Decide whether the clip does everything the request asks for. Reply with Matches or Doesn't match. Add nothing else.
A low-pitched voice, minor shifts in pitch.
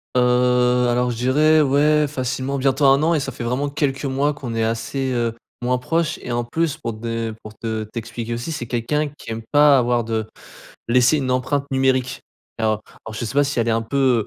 Doesn't match